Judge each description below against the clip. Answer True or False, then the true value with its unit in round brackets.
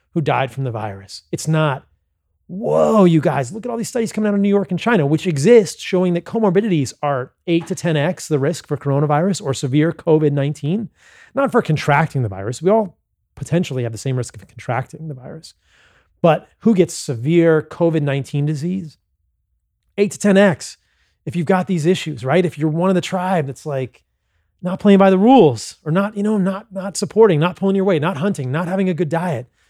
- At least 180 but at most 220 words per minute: True (200 wpm)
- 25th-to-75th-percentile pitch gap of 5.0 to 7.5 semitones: True (5.5 semitones)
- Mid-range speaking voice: True (165 Hz)